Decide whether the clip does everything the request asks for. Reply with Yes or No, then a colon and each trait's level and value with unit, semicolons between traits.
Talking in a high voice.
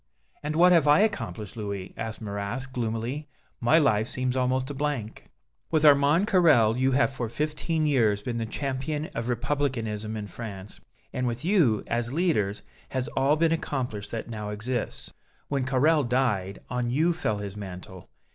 No: low, 125 Hz